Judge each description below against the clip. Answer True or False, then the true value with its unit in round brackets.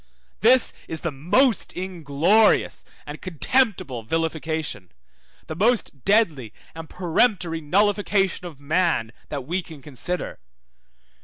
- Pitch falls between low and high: True (165 Hz)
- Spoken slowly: True (105 wpm)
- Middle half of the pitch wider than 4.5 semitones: True (5.1 semitones)